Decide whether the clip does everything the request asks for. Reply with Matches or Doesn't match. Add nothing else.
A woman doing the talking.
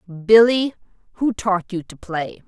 Matches